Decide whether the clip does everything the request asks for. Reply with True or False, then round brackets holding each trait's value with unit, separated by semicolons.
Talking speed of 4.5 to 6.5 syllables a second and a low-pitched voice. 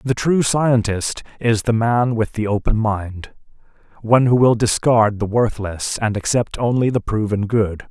False (4.3 syllables/s; 110 Hz)